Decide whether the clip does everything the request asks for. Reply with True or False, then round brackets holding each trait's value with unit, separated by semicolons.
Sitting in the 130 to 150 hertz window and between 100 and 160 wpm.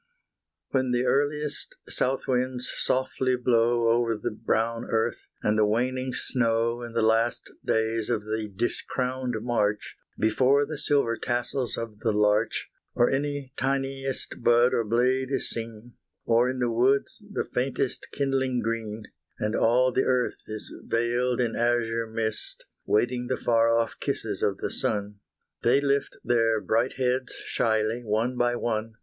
False (120 Hz; 150 wpm)